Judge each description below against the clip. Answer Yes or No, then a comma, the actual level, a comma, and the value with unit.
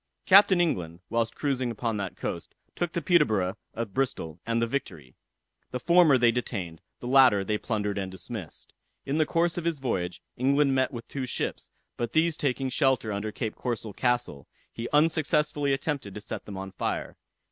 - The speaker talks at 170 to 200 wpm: Yes, average, 180 wpm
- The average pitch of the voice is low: Yes, low, 125 Hz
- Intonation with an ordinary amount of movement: No, wide, 6.0 semitones